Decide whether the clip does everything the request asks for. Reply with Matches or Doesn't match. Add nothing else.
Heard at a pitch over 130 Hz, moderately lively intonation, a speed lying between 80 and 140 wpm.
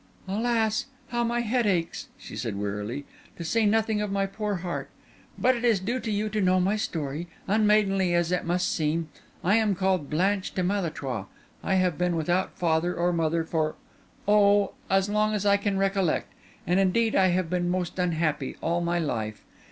Doesn't match